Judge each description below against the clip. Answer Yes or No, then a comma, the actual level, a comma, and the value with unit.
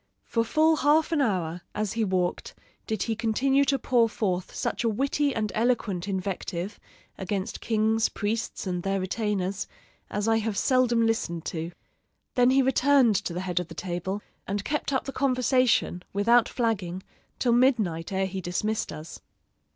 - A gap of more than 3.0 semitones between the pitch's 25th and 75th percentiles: Yes, average, 4.7 semitones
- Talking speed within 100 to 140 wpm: No, average, 165 wpm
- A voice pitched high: Yes, high, 215 Hz